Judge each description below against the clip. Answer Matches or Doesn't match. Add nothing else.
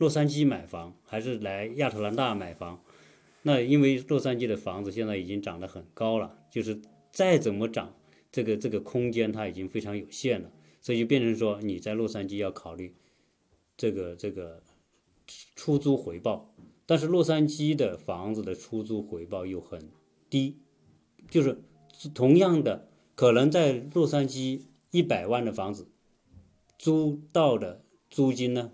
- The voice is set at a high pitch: Doesn't match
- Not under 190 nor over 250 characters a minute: Matches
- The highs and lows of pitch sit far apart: Matches